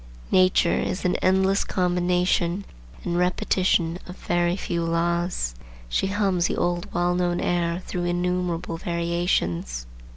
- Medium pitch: Yes, medium, 175 Hz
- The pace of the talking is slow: Yes, slow, 130 wpm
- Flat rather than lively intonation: Yes, narrow, 1.0 semitones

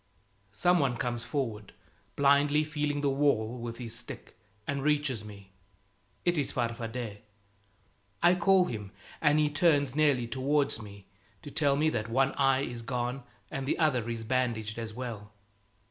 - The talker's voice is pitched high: No, low, 130 Hz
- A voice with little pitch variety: No, average, 4.1 semitones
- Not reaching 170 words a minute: Yes, average, 155 wpm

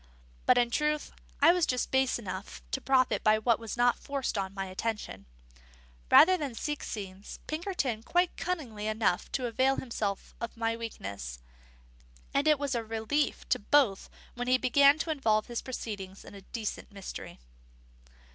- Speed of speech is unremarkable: Yes, average, 165 wpm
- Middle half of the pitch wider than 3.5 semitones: Yes, average, 4.7 semitones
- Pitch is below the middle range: No, high, 235 Hz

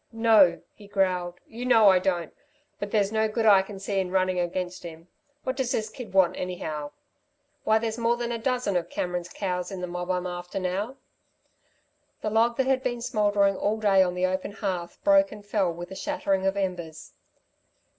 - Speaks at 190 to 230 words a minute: Yes, average, 195 wpm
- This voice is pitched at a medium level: No, high, 195 Hz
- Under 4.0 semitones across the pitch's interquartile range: Yes, average, 3.5 semitones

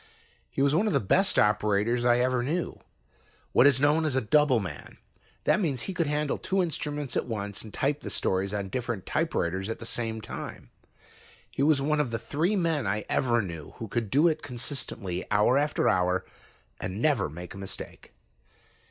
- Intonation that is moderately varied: No, wide, 6.4 semitones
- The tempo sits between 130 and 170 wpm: No, average, 190 wpm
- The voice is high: No, low, 125 Hz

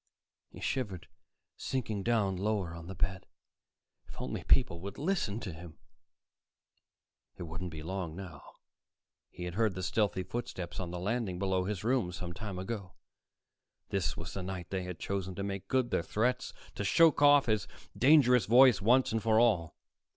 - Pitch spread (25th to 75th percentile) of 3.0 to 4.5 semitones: Yes, average, 4.2 semitones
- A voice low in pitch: Yes, low, 100 Hz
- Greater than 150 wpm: Yes, average, 170 wpm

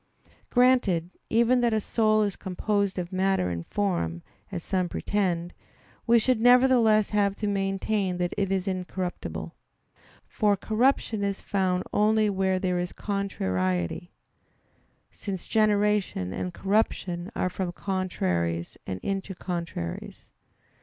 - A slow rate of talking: Yes, slow, 125 wpm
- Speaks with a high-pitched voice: Yes, high, 195 Hz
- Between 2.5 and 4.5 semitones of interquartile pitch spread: Yes, average, 3.1 semitones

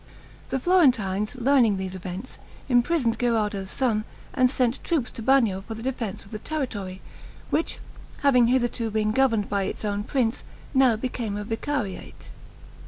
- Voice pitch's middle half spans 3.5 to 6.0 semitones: Yes, average, 4.0 semitones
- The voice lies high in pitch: Yes, high, 230 Hz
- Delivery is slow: No, average, 150 wpm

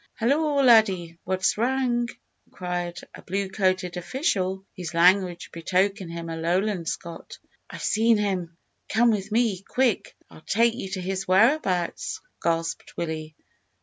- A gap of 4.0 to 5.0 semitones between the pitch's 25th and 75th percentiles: Yes, average, 4.3 semitones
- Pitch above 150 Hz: Yes, high, 190 Hz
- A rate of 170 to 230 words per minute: No, slow, 135 wpm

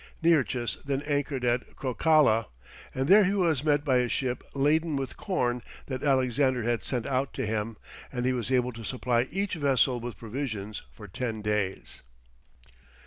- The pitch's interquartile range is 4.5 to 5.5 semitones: No, average, 3.3 semitones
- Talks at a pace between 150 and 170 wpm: Yes, average, 165 wpm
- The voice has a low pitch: Yes, low, 130 Hz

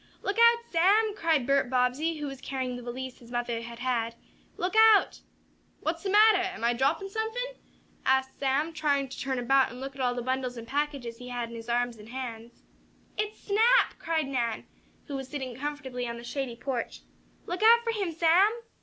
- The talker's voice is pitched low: No, very high, 270 Hz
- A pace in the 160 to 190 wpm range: No, average, 200 wpm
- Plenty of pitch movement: Yes, wide, 6.0 semitones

